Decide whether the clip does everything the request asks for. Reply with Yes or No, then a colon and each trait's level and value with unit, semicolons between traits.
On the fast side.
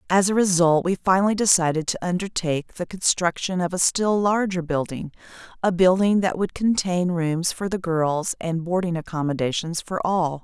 No: average, 160 wpm